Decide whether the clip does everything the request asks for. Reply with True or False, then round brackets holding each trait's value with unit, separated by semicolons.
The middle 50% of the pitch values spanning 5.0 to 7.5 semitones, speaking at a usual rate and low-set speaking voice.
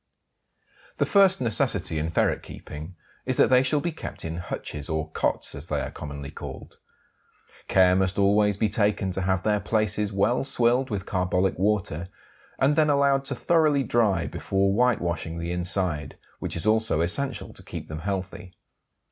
True (5.4 semitones; 165 wpm; 100 Hz)